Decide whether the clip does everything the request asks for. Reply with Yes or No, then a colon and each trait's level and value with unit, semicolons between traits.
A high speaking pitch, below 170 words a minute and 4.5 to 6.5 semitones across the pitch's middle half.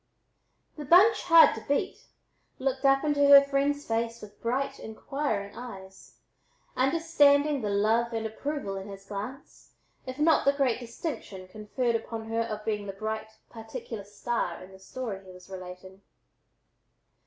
Yes: high, 230 Hz; average, 150 wpm; wide, 5.5 semitones